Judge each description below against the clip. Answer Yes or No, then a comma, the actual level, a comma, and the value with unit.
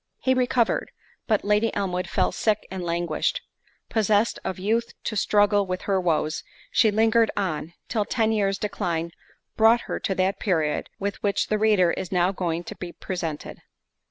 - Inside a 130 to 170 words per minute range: Yes, average, 160 wpm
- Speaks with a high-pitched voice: Yes, high, 200 Hz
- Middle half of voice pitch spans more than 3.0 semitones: Yes, average, 3.4 semitones